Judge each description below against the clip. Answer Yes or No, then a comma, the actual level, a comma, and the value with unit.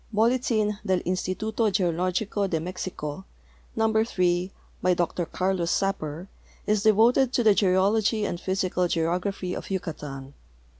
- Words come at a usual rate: No, slow, 120 wpm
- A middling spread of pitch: Yes, average, 3.3 semitones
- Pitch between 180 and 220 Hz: Yes, high, 190 Hz